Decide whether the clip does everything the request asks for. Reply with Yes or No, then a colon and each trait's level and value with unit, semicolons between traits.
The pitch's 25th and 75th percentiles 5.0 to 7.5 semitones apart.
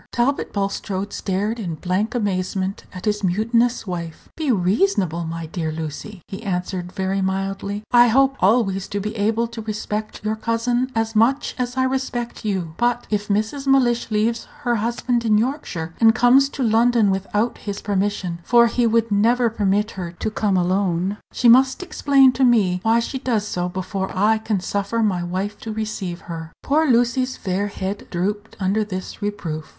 No: average, 3.8 semitones